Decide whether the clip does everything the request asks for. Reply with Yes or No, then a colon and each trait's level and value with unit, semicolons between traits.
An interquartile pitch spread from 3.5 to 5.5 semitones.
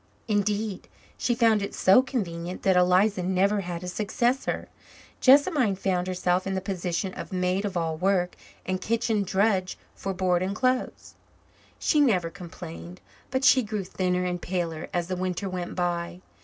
No: average, 2.8 semitones